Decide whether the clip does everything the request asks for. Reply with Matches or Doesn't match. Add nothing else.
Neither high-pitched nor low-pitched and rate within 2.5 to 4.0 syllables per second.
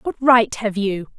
Doesn't match